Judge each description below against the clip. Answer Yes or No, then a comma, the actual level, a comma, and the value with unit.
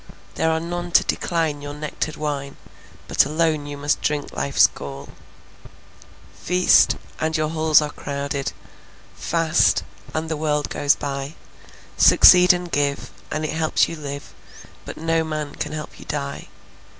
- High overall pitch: No, medium, 150 Hz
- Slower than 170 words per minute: Yes, average, 150 wpm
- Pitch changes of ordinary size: No, narrow, 2.0 semitones